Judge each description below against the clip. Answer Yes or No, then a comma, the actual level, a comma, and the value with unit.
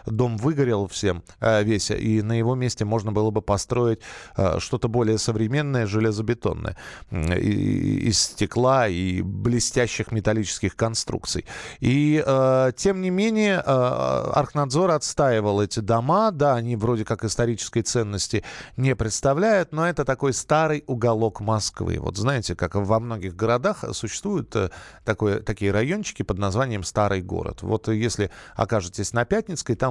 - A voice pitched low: Yes, low, 115 Hz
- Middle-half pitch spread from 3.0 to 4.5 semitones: Yes, average, 3.9 semitones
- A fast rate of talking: No, average, 135 wpm